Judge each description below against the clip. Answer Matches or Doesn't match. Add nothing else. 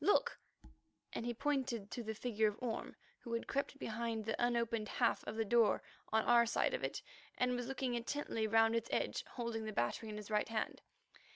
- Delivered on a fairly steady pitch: Matches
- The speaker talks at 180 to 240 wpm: Matches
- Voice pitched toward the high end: Matches